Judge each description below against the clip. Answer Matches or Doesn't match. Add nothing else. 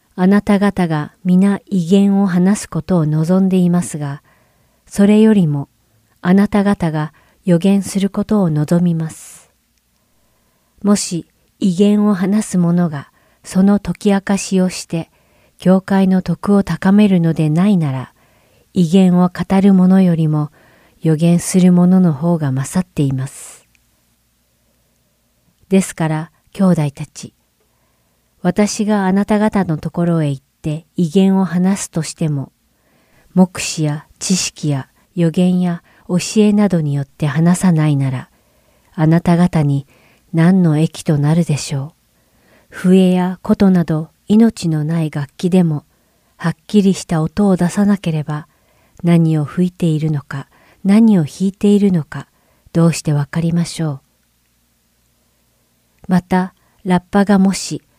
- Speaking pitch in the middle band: Matches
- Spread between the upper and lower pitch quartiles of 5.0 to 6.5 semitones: Doesn't match